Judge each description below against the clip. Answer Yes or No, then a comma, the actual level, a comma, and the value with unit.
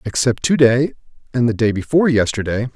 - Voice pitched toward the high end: No, low, 125 Hz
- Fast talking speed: No, average, 175 wpm